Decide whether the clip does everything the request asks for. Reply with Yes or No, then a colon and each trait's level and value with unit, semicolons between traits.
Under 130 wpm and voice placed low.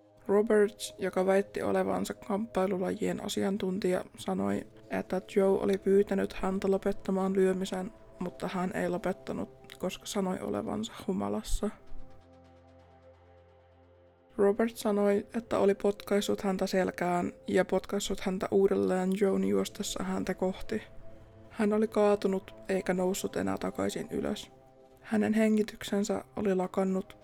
No: average, 110 wpm; medium, 185 Hz